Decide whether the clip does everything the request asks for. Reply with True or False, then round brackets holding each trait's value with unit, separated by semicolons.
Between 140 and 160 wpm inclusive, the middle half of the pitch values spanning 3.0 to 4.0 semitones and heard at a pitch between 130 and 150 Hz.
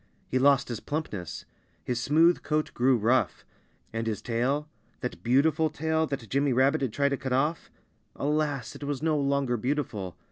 False (170 wpm; 3.5 semitones; 140 Hz)